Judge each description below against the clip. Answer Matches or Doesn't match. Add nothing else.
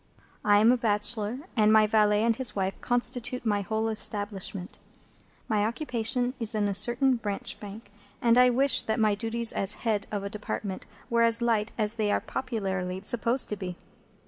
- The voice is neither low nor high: Doesn't match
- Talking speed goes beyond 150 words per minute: Matches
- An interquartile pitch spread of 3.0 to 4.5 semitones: Doesn't match